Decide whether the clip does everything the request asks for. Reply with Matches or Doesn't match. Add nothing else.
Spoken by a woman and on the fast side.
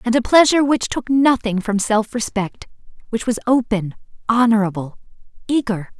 Doesn't match